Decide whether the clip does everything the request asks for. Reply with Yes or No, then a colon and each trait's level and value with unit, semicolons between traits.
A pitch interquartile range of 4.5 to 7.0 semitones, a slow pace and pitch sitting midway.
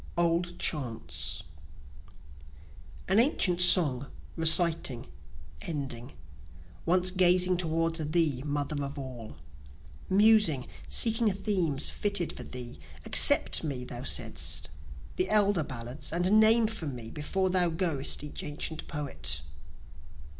Yes: average, 5.2 semitones; slow, 110 wpm; medium, 165 Hz